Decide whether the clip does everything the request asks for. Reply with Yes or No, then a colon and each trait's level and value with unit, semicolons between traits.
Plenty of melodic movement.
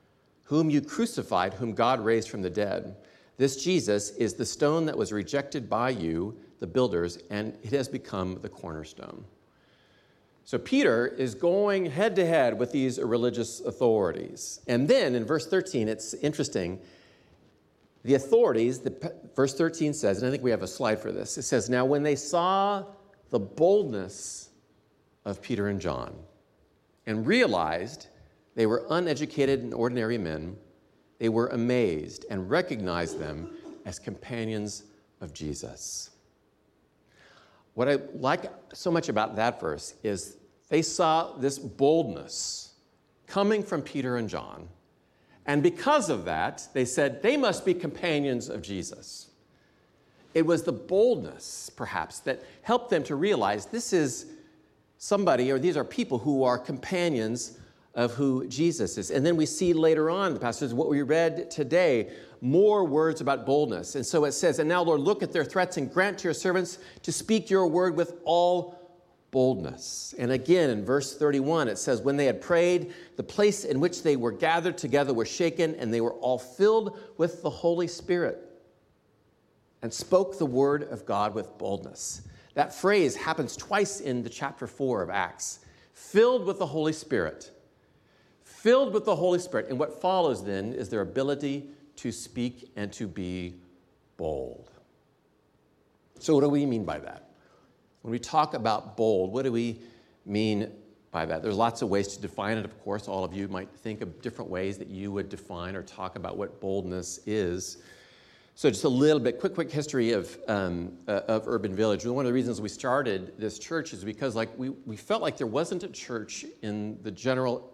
Yes: wide, 7.4 semitones